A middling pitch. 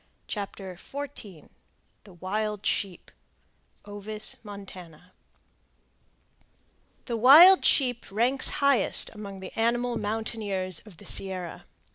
No: high, 210 Hz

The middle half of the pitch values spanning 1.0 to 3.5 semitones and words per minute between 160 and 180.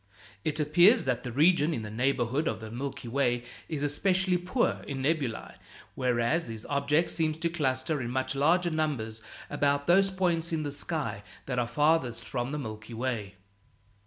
No: average, 5.0 semitones; average, 170 wpm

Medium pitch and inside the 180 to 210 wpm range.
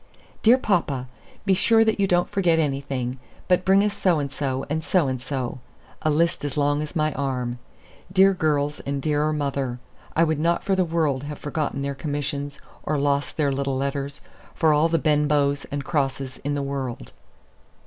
Yes: medium, 145 Hz; average, 185 wpm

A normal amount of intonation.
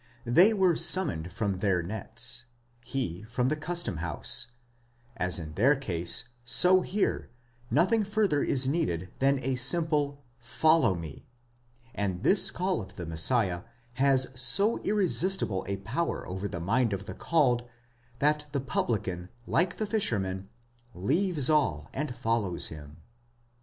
No: wide, 8.9 semitones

